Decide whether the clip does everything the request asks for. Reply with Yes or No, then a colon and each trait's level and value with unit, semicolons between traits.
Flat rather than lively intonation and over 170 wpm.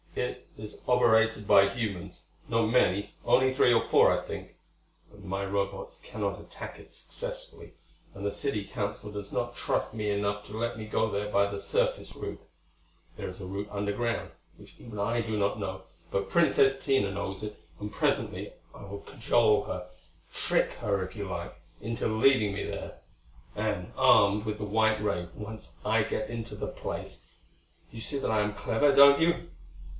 Yes: narrow, 2.3 semitones; average, 180 wpm